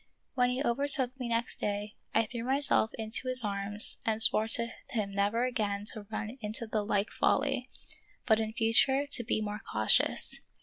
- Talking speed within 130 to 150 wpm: No, average, 175 wpm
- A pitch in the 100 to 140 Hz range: No, high, 225 Hz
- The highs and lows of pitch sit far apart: No, average, 3.0 semitones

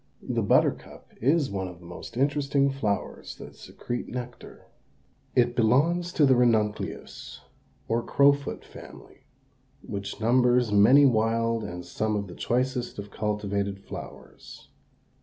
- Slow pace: Yes, slow, 125 wpm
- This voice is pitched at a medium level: No, low, 120 Hz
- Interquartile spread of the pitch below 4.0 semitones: No, average, 4.3 semitones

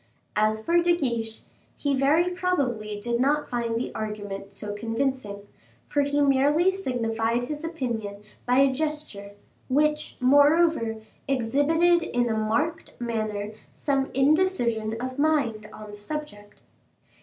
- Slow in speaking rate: Yes, slow, 130 wpm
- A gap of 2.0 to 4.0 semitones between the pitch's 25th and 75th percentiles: No, wide, 5.4 semitones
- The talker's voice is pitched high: Yes, very high, 255 Hz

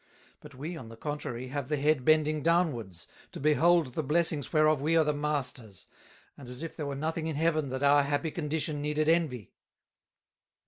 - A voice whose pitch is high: No, medium, 150 Hz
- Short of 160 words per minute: No, average, 185 wpm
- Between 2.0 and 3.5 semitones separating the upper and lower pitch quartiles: Yes, narrow, 2.6 semitones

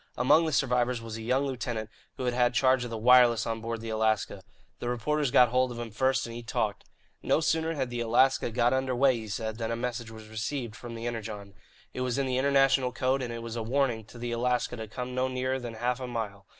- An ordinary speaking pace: No, fast, 245 wpm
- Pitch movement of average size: No, narrow, 2.2 semitones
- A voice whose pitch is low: Yes, low, 120 Hz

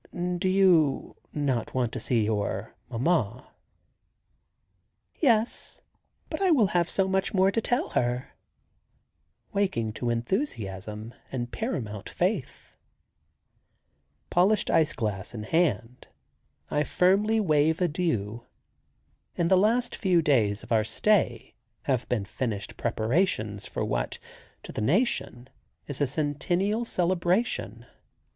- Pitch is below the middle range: No, medium, 145 Hz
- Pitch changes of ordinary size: No, wide, 8.5 semitones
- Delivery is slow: Yes, slow, 115 wpm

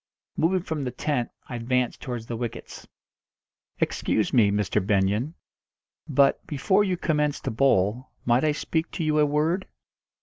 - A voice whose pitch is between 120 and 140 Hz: Yes, low, 135 Hz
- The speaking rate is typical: Yes, average, 155 wpm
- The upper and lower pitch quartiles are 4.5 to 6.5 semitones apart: Yes, average, 5.0 semitones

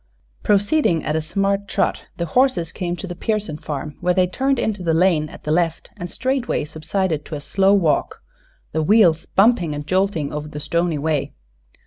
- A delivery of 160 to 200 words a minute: Yes, average, 185 wpm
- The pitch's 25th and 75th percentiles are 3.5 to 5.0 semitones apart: Yes, average, 4.3 semitones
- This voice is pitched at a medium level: Yes, medium, 175 Hz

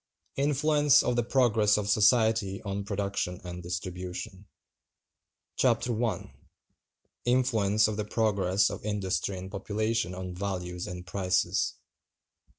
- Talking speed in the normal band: No, slow, 115 wpm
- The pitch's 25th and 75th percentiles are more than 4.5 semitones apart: No, average, 3.3 semitones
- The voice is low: Yes, low, 100 Hz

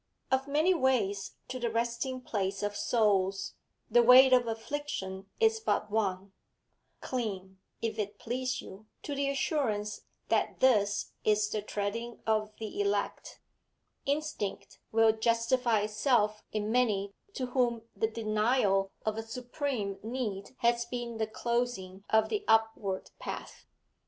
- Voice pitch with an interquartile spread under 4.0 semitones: Yes, average, 3.4 semitones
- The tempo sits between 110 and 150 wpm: Yes, slow, 135 wpm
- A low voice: No, high, 225 Hz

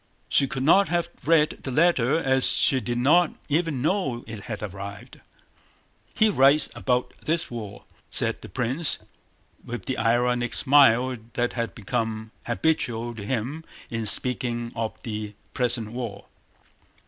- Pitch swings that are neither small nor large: Yes, average, 3.8 semitones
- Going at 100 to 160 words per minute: Yes, average, 140 wpm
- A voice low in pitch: Yes, low, 125 Hz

